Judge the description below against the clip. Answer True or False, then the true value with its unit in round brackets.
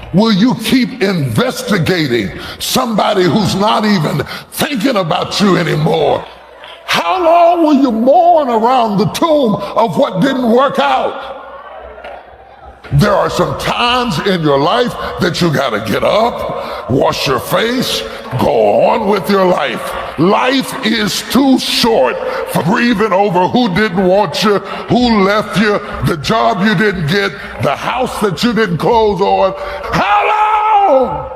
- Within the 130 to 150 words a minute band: True (140 wpm)